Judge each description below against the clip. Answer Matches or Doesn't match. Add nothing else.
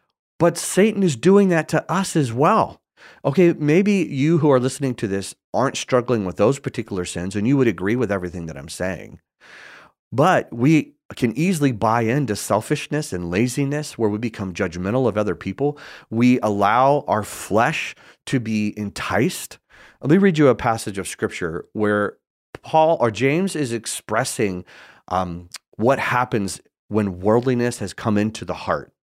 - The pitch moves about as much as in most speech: Doesn't match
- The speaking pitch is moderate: Doesn't match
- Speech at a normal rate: Matches